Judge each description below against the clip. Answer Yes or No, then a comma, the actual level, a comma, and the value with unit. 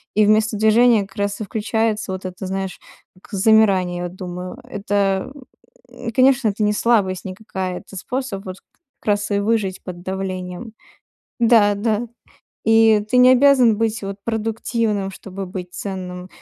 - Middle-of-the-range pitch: No, high, 205 Hz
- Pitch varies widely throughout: No, average, 2.9 semitones